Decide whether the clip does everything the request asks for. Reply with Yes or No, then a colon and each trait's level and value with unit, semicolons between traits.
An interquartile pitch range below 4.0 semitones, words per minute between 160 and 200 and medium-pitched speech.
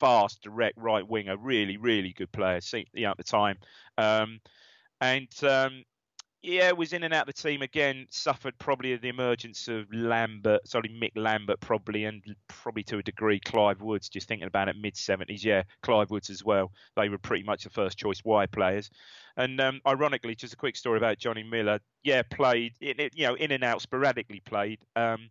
No: average, 3.3 semitones; average, 190 wpm; low, 110 Hz